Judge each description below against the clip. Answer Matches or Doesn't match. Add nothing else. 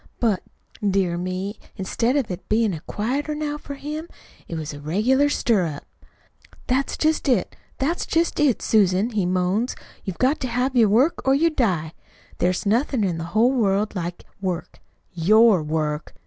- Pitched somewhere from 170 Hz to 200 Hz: Doesn't match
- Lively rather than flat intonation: Matches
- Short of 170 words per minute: Matches